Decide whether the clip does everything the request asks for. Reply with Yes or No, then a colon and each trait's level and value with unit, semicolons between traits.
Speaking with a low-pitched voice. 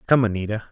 Yes: low, 110 Hz